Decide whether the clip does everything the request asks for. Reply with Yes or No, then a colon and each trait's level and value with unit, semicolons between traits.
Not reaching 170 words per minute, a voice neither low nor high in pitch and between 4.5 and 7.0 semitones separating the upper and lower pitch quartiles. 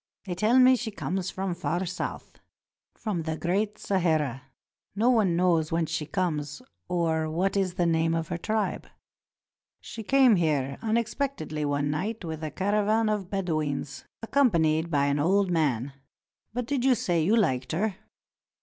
Yes: average, 160 wpm; medium, 175 Hz; average, 5.2 semitones